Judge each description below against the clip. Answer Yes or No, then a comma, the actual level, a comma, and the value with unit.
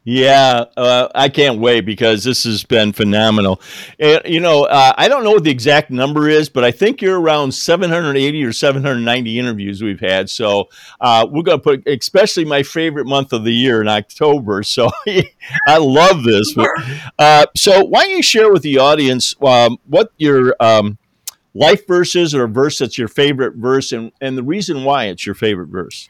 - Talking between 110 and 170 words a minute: No, average, 195 wpm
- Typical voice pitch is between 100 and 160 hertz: Yes, low, 135 Hz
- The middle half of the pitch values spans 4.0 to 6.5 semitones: Yes, average, 4.6 semitones